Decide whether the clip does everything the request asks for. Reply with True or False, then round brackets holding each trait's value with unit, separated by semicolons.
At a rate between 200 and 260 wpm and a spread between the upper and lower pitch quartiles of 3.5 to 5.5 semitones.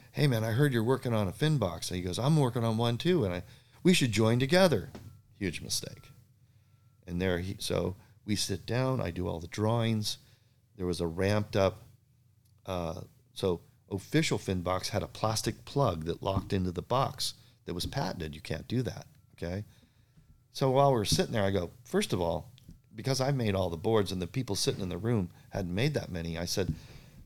True (205 wpm; 4.9 semitones)